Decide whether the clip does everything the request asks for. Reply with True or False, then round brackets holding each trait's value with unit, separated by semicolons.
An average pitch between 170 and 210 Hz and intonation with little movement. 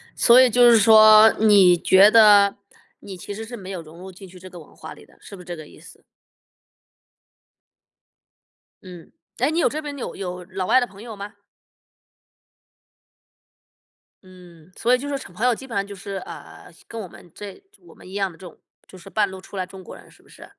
False (200 Hz; 3.3 semitones)